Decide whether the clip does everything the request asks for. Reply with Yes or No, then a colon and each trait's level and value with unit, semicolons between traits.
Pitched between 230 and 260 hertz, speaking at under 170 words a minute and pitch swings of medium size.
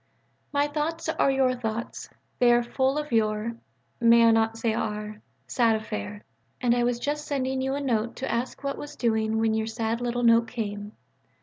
No: high, 235 Hz; average, 195 wpm; average, 3.0 semitones